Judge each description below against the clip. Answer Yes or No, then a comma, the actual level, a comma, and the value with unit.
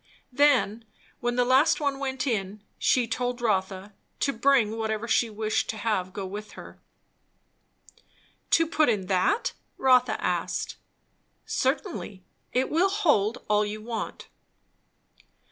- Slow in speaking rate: Yes, slow, 130 wpm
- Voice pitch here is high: Yes, high, 235 Hz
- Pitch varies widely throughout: No, average, 4.1 semitones